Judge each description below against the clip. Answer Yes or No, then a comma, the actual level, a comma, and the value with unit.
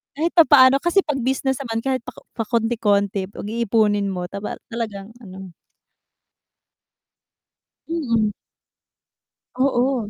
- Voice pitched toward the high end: Yes, high, 230 Hz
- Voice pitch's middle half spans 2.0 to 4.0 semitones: No, average, 4.4 semitones